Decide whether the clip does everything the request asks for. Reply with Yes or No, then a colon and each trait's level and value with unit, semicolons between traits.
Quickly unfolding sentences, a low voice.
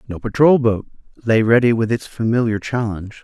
No: average, 165 wpm; low, 115 Hz